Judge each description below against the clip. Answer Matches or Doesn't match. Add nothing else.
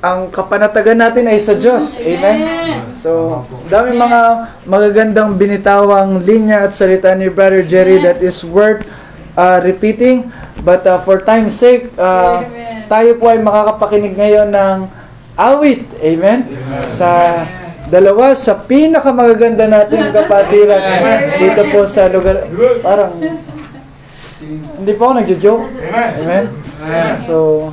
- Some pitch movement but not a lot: Matches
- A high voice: Matches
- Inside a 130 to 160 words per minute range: Doesn't match